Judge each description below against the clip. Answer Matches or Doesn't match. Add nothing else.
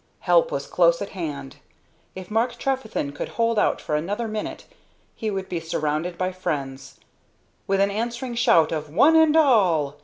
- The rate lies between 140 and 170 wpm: Matches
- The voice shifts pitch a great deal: Matches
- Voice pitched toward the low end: Doesn't match